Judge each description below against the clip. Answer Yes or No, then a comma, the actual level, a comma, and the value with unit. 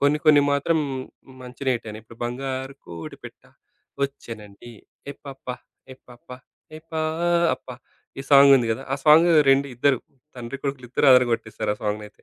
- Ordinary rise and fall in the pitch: Yes, average, 3.1 semitones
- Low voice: Yes, low, 130 Hz